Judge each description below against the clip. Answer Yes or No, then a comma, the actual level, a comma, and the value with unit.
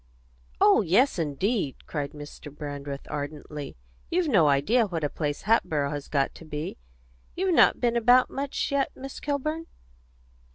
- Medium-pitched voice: Yes, medium, 165 Hz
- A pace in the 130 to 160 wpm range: Yes, average, 150 wpm